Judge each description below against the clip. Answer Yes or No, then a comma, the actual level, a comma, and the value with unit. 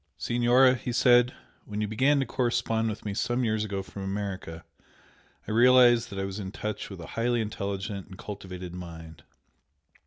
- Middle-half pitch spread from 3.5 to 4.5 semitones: Yes, average, 3.8 semitones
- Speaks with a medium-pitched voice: No, low, 105 Hz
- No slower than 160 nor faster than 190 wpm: Yes, average, 175 wpm